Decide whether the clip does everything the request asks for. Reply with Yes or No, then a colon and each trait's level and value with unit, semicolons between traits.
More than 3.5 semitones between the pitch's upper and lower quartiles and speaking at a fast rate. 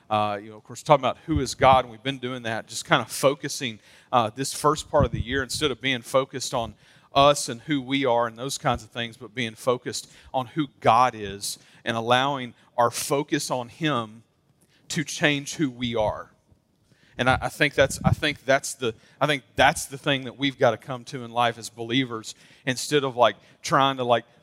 No: average, 3.2 semitones; fast, 220 wpm